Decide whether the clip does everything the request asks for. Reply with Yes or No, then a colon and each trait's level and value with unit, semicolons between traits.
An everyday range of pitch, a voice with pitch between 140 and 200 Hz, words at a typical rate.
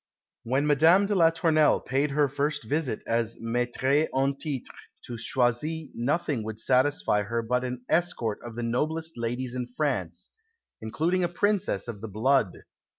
No: average, 4.9 semitones; low, 130 Hz; average, 155 wpm